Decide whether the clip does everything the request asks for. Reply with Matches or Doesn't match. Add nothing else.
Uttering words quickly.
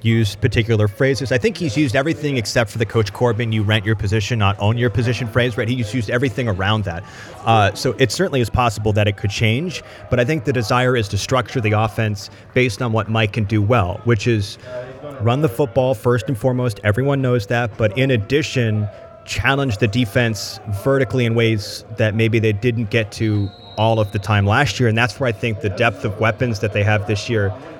Matches